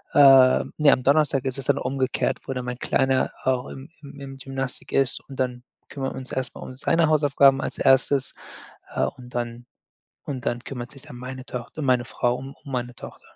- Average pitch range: No, narrow, 1.6 semitones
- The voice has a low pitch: Yes, low, 130 Hz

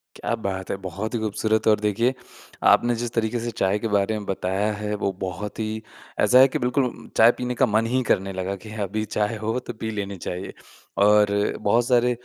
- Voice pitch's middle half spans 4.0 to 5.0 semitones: No, average, 2.8 semitones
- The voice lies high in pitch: No, low, 110 Hz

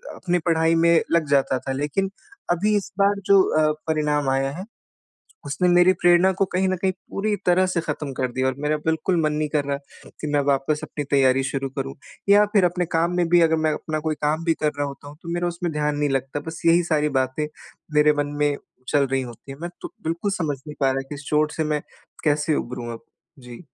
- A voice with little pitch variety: No, average, 3.6 semitones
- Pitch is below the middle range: No, medium, 155 Hz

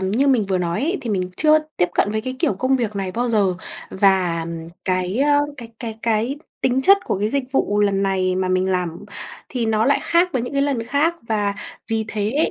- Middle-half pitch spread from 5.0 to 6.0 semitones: Yes, wide, 5.6 semitones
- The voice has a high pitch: Yes, high, 215 Hz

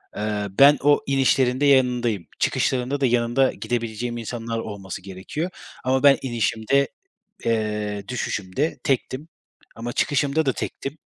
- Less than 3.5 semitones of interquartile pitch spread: No, average, 3.9 semitones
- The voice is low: Yes, low, 120 Hz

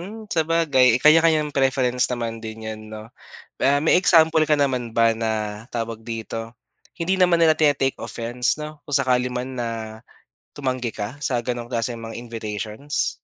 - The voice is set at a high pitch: No, low, 125 Hz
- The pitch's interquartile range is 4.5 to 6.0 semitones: Yes, average, 4.8 semitones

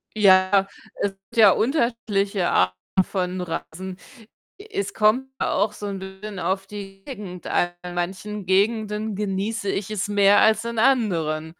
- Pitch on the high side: Yes, high, 200 Hz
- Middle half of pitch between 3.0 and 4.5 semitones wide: No, narrow, 2.4 semitones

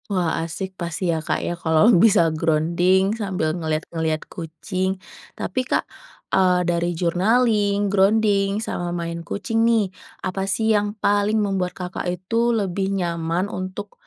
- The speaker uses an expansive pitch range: No, average, 3.2 semitones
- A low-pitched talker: No, medium, 185 Hz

